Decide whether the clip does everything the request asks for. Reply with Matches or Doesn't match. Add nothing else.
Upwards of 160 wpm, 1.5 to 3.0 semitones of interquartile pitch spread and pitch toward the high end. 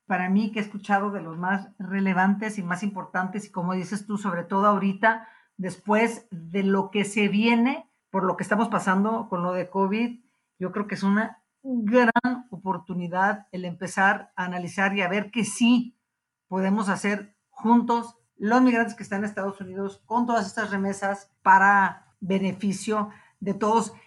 Matches